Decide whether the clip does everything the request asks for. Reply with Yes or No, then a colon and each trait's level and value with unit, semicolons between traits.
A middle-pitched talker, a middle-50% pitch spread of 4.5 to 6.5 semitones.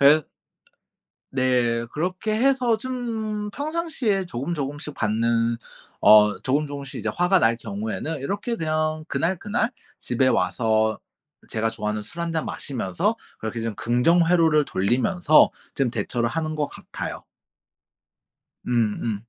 No: medium, 150 Hz; wide, 7.9 semitones